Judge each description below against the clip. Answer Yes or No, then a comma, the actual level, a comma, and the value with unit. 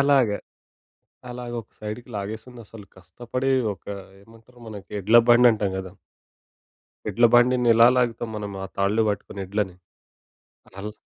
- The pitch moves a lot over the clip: No, average, 3.1 semitones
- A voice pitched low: Yes, low, 110 Hz